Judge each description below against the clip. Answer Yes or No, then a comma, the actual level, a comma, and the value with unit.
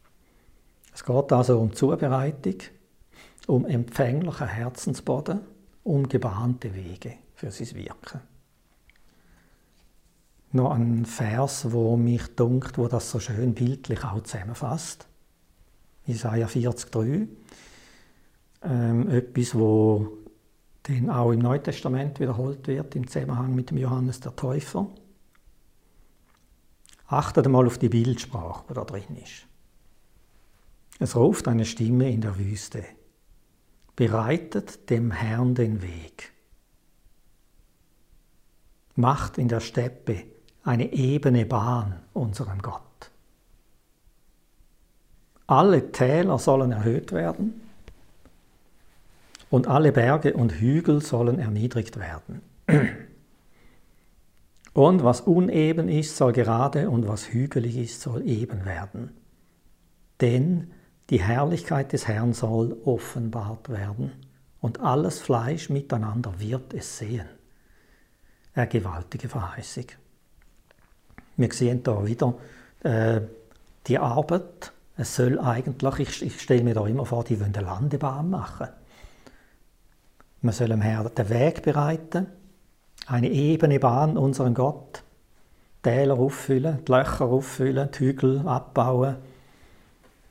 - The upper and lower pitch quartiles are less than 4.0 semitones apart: Yes, average, 3.2 semitones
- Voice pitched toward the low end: Yes, low, 125 Hz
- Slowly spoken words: Yes, slow, 105 wpm